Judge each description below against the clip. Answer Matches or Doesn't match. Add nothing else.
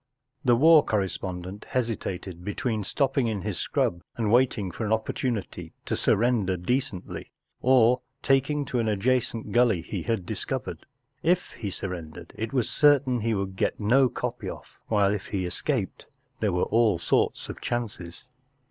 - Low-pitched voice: Matches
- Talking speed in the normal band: Matches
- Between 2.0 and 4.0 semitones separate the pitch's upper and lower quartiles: Doesn't match